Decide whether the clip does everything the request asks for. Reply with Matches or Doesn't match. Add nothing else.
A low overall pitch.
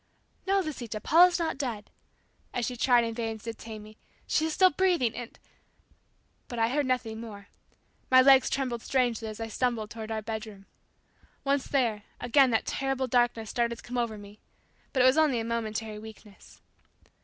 Doesn't match